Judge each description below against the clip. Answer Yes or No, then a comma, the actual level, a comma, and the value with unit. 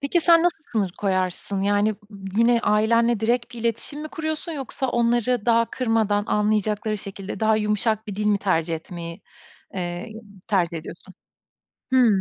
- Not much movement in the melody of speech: No, average, 3.2 semitones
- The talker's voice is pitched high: Yes, high, 215 Hz